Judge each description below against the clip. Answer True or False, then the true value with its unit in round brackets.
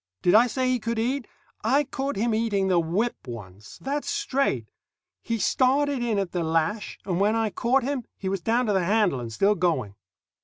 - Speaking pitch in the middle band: False (220 Hz)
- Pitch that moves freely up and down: True (6.1 semitones)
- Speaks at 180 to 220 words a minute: True (200 wpm)